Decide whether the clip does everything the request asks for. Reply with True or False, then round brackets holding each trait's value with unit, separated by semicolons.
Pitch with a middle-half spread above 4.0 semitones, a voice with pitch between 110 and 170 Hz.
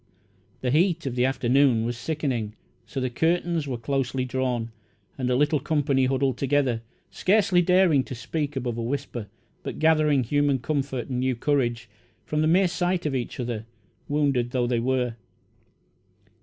False (3.6 semitones; 135 Hz)